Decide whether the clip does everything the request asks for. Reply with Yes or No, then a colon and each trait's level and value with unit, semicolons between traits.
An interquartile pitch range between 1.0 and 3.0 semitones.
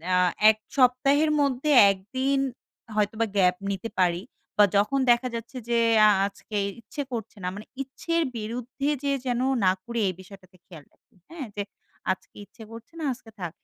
No: average, 4.7 semitones